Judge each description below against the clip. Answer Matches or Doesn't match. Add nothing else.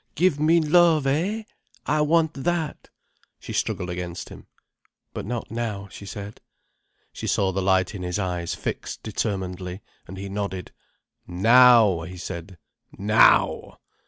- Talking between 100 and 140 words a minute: Matches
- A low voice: Matches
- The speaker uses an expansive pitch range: Matches